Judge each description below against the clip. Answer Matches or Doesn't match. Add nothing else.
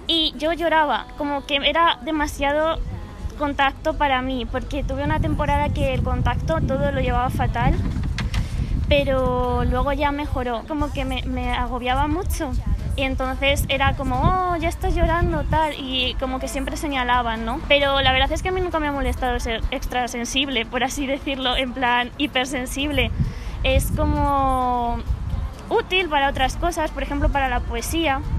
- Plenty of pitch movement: Doesn't match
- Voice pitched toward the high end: Matches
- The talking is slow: Doesn't match